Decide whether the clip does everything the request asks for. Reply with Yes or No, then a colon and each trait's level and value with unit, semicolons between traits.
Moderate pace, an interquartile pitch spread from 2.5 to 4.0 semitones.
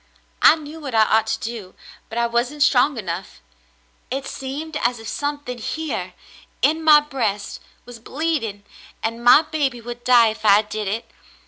No: average, 165 wpm; average, 4.8 semitones